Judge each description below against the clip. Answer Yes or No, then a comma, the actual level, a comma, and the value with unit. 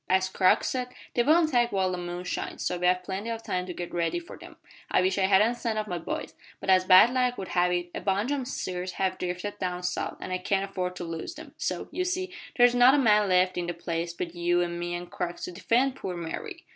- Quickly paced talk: Yes, fast, 260 wpm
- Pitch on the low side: No, medium, 185 Hz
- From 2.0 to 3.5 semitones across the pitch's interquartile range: No, average, 4.6 semitones